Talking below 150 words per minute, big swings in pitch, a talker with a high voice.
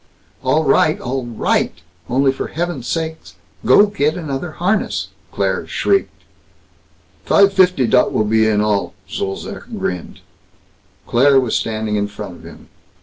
No: average, 140 wpm; wide, 6.9 semitones; low, 135 Hz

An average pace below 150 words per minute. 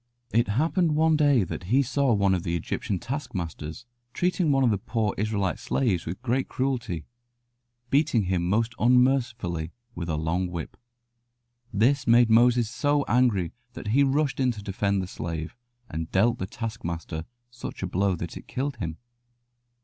No: average, 165 wpm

